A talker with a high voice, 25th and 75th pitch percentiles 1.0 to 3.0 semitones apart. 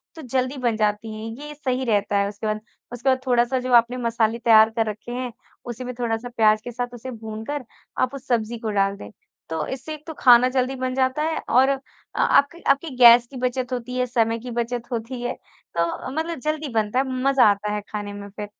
Yes: high, 240 Hz; average, 2.7 semitones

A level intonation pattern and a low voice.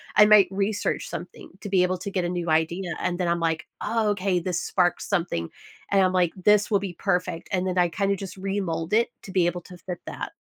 No: narrow, 2.2 semitones; medium, 185 Hz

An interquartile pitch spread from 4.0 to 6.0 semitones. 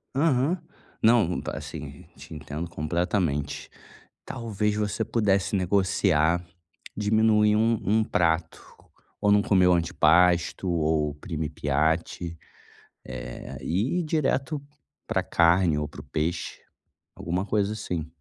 Yes: average, 4.8 semitones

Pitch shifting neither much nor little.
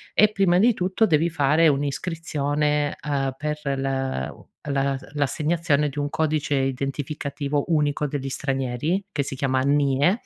No: narrow, 2.3 semitones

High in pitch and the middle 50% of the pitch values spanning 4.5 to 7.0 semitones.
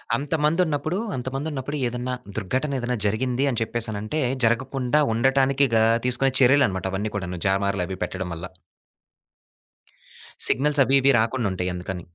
No: low, 125 Hz; average, 5.2 semitones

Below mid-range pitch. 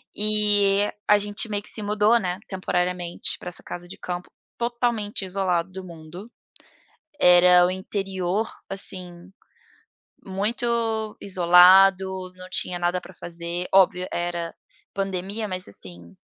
No: medium, 185 Hz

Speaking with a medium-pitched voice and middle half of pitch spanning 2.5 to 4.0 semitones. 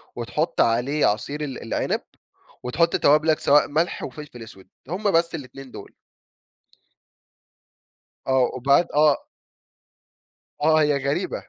Yes: medium, 145 Hz; average, 3.5 semitones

